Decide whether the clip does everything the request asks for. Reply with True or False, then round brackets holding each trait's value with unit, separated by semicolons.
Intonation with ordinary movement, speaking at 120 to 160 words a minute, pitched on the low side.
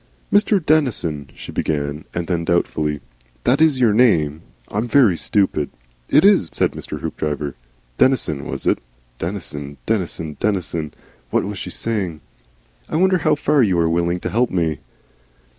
False (8.2 semitones; 155 wpm; 90 Hz)